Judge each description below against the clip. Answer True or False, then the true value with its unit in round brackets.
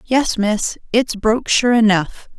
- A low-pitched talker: False (225 Hz)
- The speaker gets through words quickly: False (150 wpm)